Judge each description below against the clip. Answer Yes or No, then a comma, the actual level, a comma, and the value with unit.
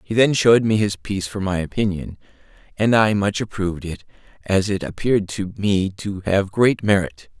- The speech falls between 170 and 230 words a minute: Yes, average, 185 wpm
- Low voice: Yes, low, 100 Hz